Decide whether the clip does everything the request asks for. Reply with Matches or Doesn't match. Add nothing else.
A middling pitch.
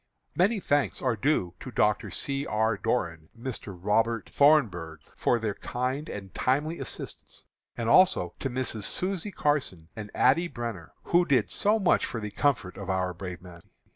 Doesn't match